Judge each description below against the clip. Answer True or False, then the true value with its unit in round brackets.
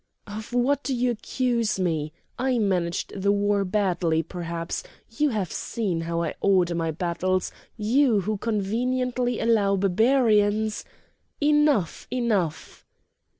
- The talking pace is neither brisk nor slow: False (120 wpm)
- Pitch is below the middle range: False (205 Hz)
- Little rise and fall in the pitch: False (5.2 semitones)